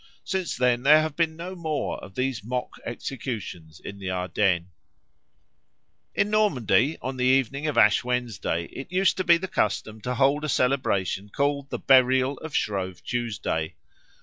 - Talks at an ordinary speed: Yes, average, 160 wpm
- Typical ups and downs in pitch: No, wide, 6.1 semitones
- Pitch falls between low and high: No, low, 125 Hz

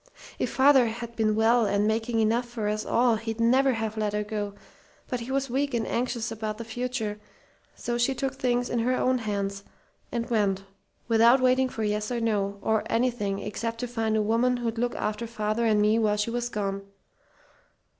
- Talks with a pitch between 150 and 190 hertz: No, high, 230 Hz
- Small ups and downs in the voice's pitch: Yes, narrow, 2.3 semitones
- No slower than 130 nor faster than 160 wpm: No, average, 195 wpm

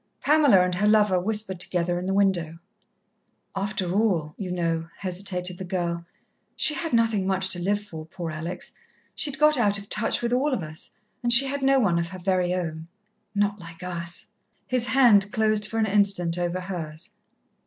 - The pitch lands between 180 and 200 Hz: Yes, high, 190 Hz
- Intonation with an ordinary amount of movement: Yes, average, 3.6 semitones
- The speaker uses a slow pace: No, average, 185 wpm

